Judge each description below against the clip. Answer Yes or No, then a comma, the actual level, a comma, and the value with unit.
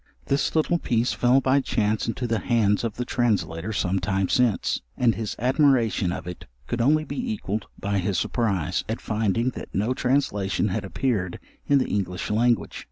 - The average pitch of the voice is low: Yes, low, 115 Hz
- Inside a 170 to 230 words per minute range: Yes, average, 175 wpm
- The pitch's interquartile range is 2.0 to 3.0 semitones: No, average, 4.3 semitones